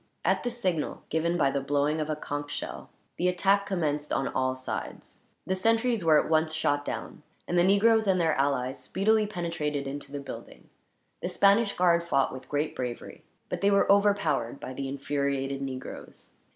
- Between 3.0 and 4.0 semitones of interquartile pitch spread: No, wide, 5.5 semitones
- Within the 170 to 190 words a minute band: Yes, average, 180 wpm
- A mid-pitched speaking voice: Yes, medium, 155 Hz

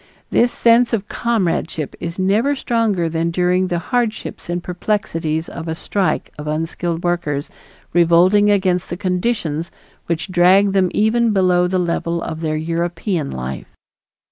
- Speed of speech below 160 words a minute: Yes, average, 140 wpm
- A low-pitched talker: No, medium, 180 Hz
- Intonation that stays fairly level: No, average, 3.5 semitones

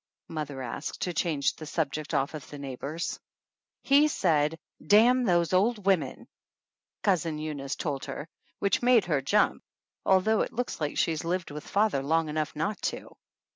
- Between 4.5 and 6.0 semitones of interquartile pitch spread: Yes, average, 5.0 semitones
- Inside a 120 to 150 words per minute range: No, average, 175 wpm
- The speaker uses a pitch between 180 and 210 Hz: No, medium, 165 Hz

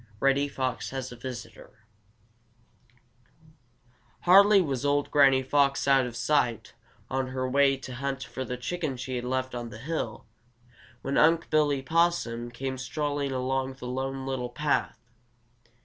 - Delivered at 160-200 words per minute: No, average, 145 wpm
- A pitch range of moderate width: No, narrow, 2.0 semitones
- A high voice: No, low, 135 Hz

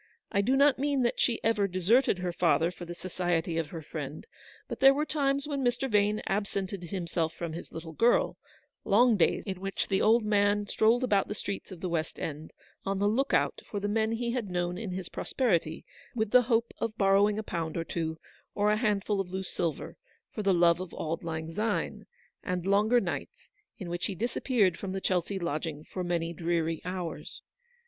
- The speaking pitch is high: Yes, high, 195 Hz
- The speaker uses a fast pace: Yes, fast, 210 wpm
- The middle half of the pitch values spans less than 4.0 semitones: No, average, 4.3 semitones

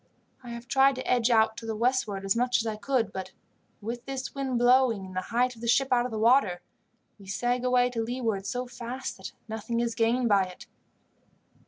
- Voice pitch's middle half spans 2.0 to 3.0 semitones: Yes, narrow, 2.5 semitones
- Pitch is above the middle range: Yes, high, 235 Hz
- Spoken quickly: Yes, fast, 210 wpm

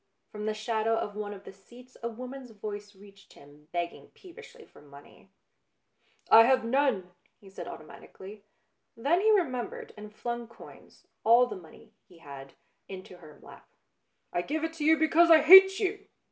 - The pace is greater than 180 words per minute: No, average, 175 wpm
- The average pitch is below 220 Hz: No, high, 225 Hz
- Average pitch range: No, wide, 6.7 semitones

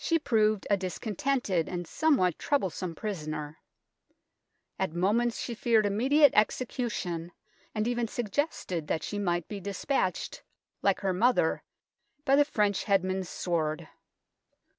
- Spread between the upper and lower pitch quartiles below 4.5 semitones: No, average, 5.1 semitones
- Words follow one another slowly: Yes, slow, 120 wpm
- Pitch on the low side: No, high, 200 Hz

